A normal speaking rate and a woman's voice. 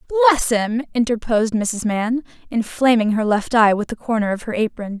Yes: average, 180 wpm; female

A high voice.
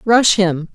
Yes: high, 195 Hz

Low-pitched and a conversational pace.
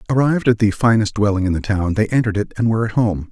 No: low, 110 Hz; fast, 270 wpm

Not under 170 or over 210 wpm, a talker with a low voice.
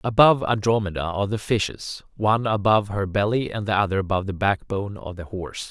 Yes: average, 190 wpm; low, 100 Hz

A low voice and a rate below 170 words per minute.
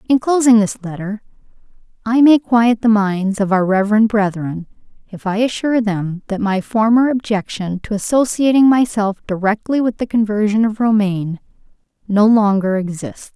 No: high, 215 Hz; average, 150 wpm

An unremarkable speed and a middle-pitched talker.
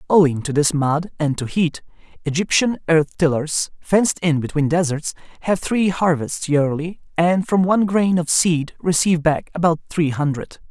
Yes: average, 165 wpm; medium, 165 Hz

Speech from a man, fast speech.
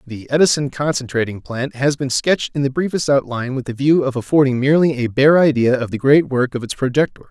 Yes: male; fast, 220 wpm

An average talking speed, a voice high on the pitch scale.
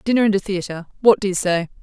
No: fast, 230 wpm; high, 195 Hz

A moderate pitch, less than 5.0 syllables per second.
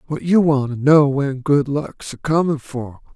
Yes: medium, 145 Hz; 4.2 syllables/s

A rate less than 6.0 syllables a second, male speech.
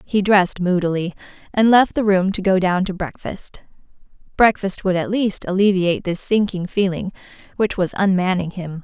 No: 5.1 syllables/s; female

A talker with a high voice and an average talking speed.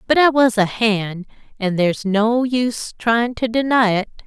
Yes: high, 225 Hz; average, 185 wpm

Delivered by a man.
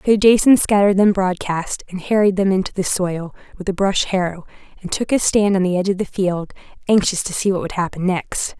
No: female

